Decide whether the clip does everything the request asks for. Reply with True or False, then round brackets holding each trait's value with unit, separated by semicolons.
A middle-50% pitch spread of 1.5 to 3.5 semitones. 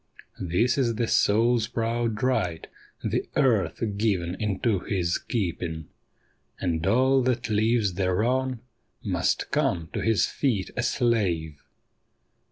False (4.7 semitones)